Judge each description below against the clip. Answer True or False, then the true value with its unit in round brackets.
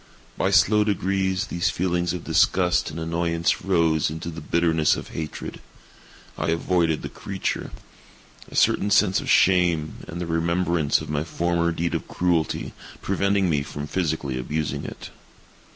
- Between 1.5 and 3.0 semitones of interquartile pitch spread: True (2.4 semitones)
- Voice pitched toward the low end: True (85 Hz)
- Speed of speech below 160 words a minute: True (150 wpm)